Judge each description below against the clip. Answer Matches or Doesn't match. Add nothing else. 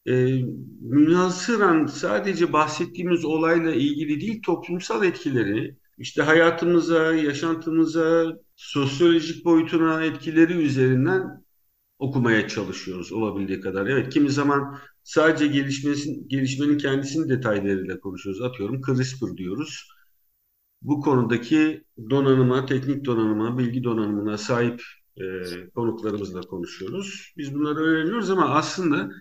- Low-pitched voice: Doesn't match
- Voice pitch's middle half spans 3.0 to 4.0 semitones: Doesn't match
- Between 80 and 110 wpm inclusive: Matches